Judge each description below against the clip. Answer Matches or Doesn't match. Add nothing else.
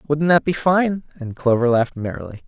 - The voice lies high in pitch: Doesn't match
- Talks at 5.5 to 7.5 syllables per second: Doesn't match